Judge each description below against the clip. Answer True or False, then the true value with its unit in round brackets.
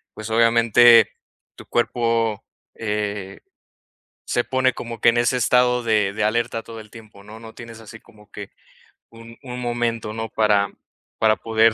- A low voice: True (115 Hz)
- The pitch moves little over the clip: True (1.6 semitones)